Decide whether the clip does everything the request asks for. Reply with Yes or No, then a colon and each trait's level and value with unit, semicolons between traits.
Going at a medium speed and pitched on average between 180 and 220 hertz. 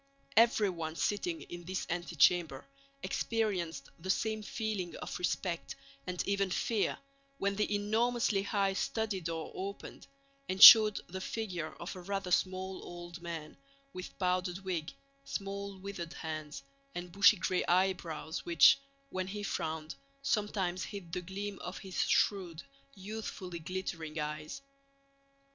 No: slow, 130 wpm; medium, 185 Hz